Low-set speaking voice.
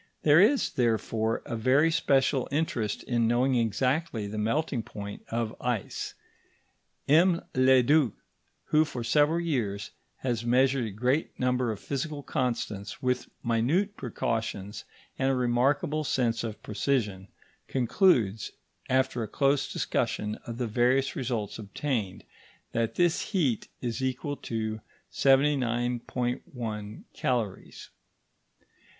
Yes: low, 125 Hz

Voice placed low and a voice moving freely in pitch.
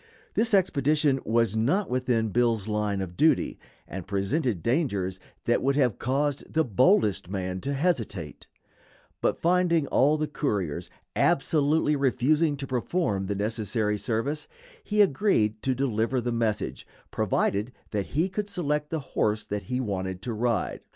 Yes: low, 125 Hz; wide, 6.1 semitones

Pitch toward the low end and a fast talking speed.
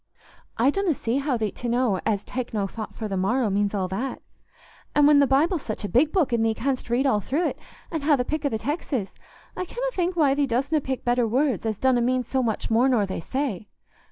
No: very high, 255 Hz; fast, 240 wpm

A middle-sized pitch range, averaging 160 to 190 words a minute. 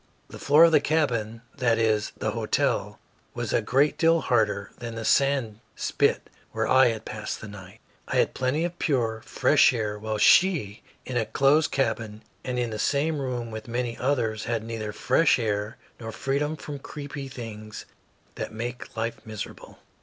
Yes: average, 4.1 semitones; average, 175 wpm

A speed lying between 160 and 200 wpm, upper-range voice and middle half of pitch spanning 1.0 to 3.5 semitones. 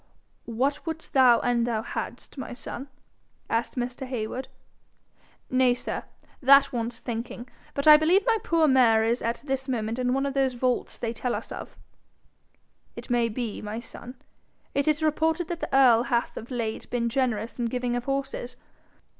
Yes: average, 170 wpm; very high, 250 Hz; narrow, 2.6 semitones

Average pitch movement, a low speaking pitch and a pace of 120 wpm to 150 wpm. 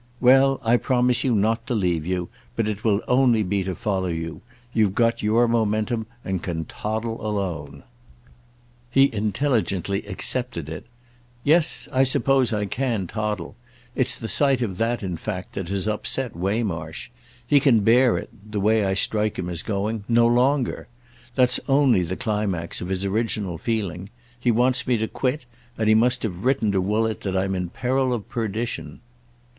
No: average, 4.1 semitones; low, 110 Hz; average, 165 wpm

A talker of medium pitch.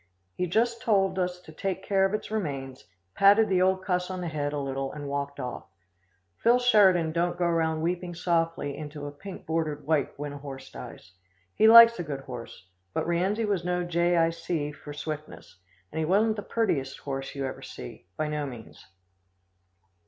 Yes: medium, 165 Hz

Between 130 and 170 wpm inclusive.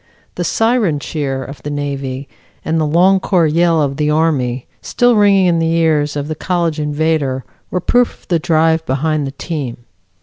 No: average, 180 wpm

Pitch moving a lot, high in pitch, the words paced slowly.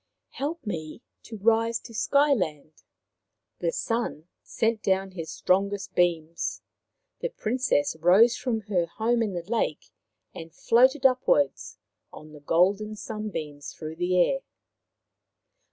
Yes: wide, 5.9 semitones; high, 200 Hz; slow, 130 wpm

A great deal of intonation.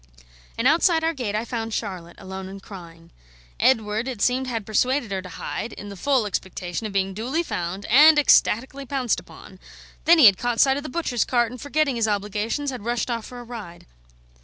No: average, 4.8 semitones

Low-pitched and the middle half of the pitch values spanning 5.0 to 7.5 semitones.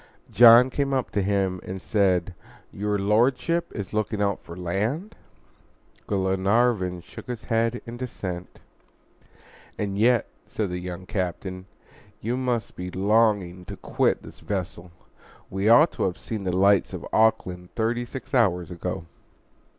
No: low, 100 Hz; average, 4.0 semitones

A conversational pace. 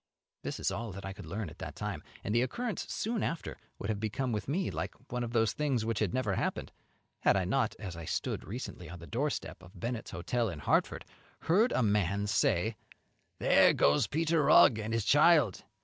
No: fast, 210 wpm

